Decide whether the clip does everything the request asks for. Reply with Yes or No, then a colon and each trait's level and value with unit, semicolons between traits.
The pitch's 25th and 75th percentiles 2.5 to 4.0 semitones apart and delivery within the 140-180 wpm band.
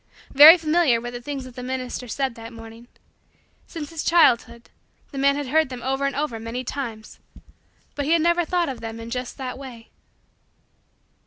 No: average, 3.7 semitones; average, 190 wpm